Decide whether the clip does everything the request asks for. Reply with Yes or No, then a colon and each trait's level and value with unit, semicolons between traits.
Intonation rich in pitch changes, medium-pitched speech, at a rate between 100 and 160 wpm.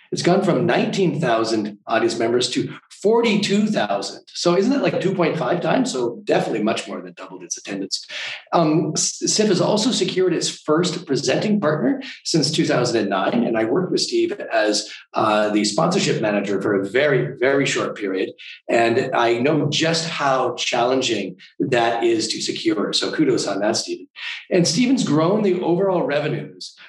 Yes: wide, 5.7 semitones; medium, 180 Hz; average, 155 wpm